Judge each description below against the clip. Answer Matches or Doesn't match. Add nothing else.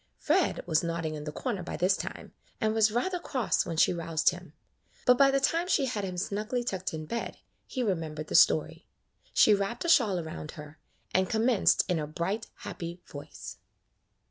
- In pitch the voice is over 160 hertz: Matches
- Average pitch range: Doesn't match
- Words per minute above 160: Matches